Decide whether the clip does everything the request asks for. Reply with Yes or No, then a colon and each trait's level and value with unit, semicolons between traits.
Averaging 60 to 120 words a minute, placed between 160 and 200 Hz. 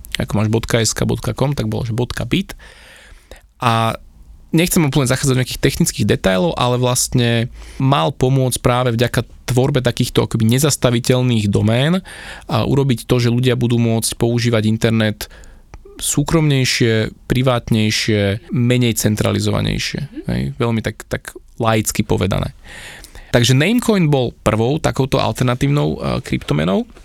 No: average, 115 wpm; low, 120 Hz